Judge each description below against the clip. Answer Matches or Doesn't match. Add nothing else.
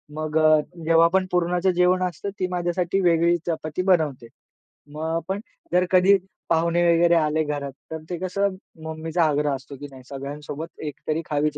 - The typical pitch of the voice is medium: Matches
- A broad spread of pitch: Doesn't match